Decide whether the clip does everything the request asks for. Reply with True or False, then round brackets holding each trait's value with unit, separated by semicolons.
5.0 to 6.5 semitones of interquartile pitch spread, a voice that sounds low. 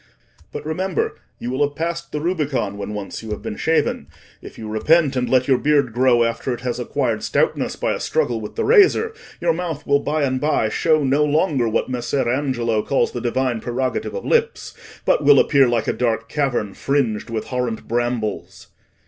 False (4.1 semitones; 130 Hz)